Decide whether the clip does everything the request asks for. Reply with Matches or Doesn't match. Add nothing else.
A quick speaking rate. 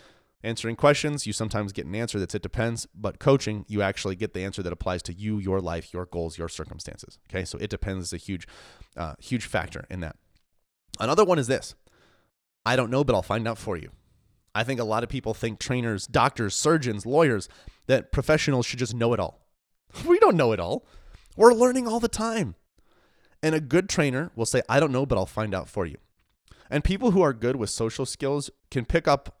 Matches